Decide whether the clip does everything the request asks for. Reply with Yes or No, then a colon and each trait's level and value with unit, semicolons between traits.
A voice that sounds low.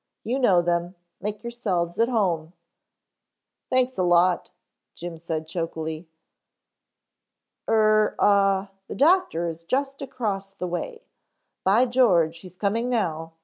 No: high, 195 Hz